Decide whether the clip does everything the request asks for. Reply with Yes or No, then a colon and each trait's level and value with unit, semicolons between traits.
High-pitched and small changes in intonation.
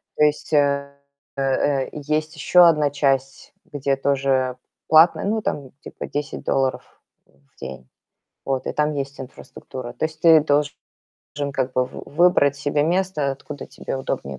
No: medium, 140 Hz; narrow, 2.2 semitones